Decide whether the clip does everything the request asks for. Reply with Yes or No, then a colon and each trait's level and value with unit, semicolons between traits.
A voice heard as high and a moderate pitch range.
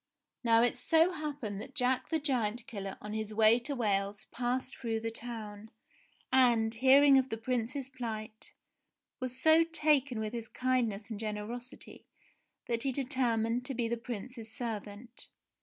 Yes: high, 235 Hz; average, 3.0 semitones